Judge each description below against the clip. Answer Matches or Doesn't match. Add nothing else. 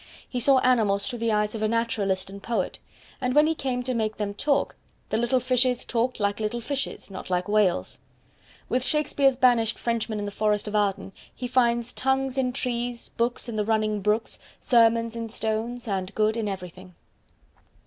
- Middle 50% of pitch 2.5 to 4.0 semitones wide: Matches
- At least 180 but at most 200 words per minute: Matches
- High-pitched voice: Matches